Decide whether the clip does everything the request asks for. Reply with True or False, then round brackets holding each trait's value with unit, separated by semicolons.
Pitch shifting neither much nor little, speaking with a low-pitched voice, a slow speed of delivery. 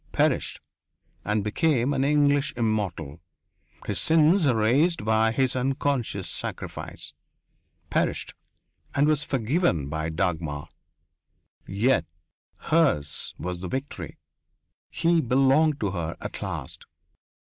False (7.4 semitones; 125 Hz; 105 wpm)